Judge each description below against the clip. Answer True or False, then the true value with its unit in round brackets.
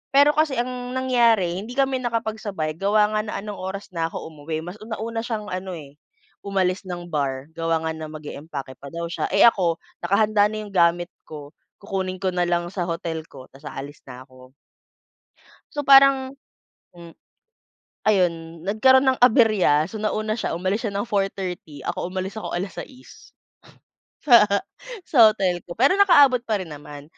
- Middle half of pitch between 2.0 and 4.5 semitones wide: False (5.0 semitones)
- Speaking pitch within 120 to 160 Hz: False (190 Hz)